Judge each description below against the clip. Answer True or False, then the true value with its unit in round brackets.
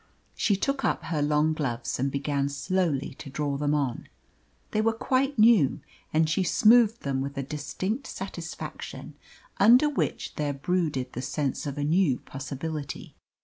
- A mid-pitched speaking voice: True (150 Hz)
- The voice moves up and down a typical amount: False (6.0 semitones)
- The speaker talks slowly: False (155 wpm)